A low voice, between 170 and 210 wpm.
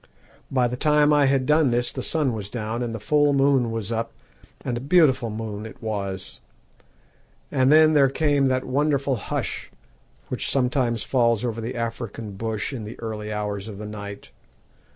Yes: low, 120 Hz; average, 175 wpm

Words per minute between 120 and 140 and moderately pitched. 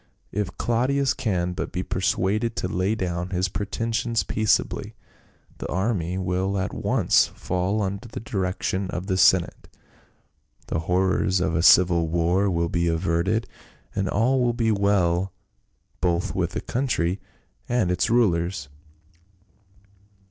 No: slow, 135 wpm; very low, 95 Hz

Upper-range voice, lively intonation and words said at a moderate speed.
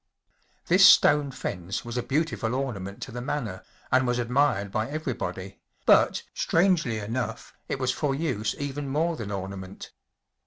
No: low, 125 Hz; wide, 5.9 semitones; average, 155 wpm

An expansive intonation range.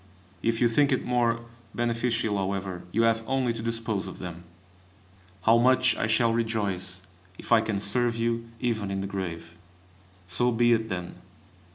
No: average, 3.2 semitones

